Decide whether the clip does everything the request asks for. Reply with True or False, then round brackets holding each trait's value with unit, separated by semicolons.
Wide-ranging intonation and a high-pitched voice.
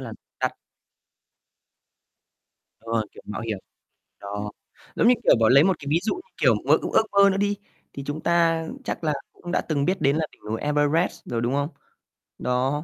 False (5.8 semitones; 150 Hz)